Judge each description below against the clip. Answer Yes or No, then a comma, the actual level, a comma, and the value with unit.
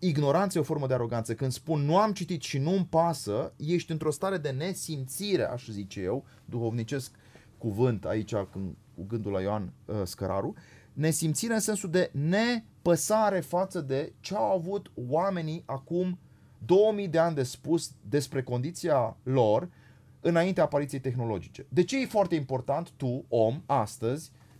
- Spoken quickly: No, average, 150 wpm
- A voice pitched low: No, medium, 145 Hz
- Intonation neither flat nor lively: No, wide, 6.2 semitones